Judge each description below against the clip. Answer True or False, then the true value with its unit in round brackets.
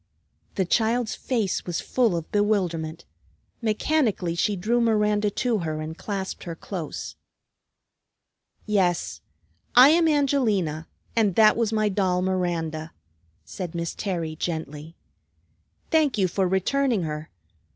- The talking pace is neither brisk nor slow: False (120 wpm)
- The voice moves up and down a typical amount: True (4.8 semitones)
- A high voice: True (195 Hz)